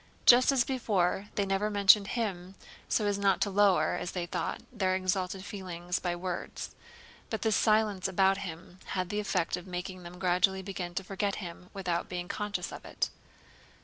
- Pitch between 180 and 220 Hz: Yes, high, 190 Hz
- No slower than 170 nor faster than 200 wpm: Yes, average, 180 wpm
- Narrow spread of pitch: Yes, narrow, 2.3 semitones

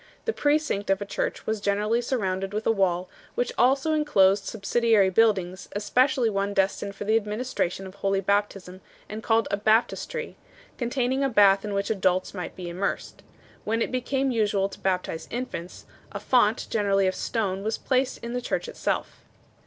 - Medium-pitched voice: No, high, 210 Hz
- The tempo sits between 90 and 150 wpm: No, average, 175 wpm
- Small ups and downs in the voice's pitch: No, average, 3.6 semitones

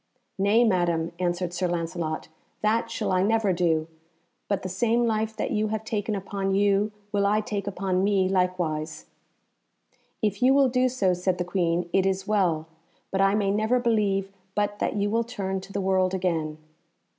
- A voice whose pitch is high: Yes, high, 195 Hz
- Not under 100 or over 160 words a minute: No, average, 180 wpm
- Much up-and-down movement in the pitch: No, average, 2.8 semitones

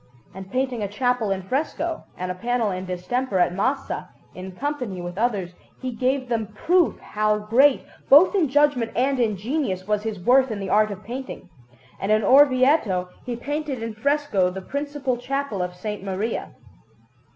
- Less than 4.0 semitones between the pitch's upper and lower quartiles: No, wide, 5.6 semitones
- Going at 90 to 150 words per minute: No, average, 175 wpm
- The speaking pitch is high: Yes, high, 230 Hz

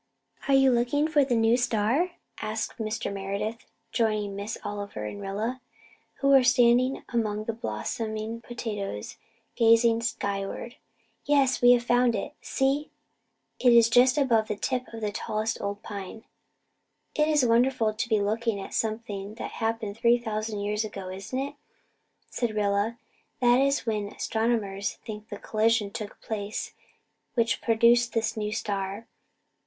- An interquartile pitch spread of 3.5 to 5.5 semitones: No, average, 2.7 semitones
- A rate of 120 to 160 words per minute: Yes, average, 145 wpm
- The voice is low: No, high, 225 Hz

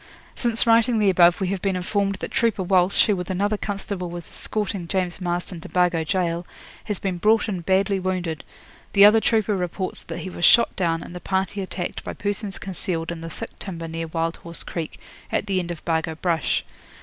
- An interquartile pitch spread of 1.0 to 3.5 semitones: Yes, average, 2.7 semitones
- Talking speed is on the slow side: No, fast, 205 wpm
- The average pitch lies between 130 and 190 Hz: Yes, medium, 185 Hz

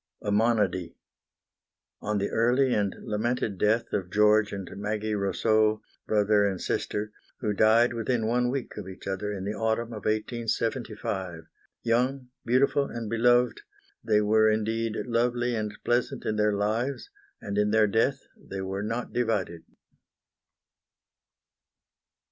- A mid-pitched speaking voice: No, low, 110 Hz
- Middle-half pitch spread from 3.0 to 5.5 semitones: No, narrow, 2.4 semitones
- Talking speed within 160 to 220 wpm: No, slow, 135 wpm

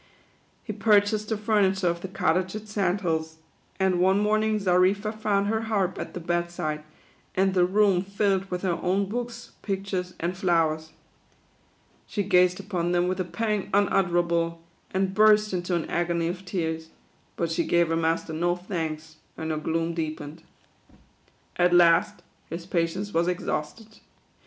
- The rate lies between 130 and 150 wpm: No, average, 160 wpm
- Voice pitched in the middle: Yes, medium, 180 Hz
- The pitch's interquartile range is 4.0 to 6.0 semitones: No, average, 3.1 semitones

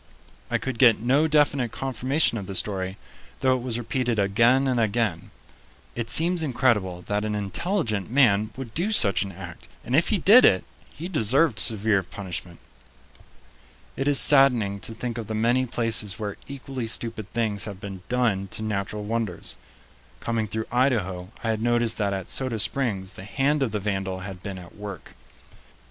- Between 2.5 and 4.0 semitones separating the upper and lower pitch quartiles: No, average, 4.5 semitones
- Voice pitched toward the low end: Yes, low, 115 Hz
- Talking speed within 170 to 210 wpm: Yes, average, 175 wpm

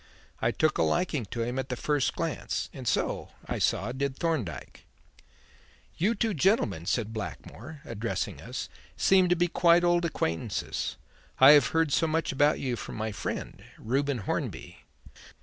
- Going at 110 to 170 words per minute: Yes, average, 160 wpm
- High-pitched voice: No, medium, 140 Hz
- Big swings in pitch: Yes, wide, 6.2 semitones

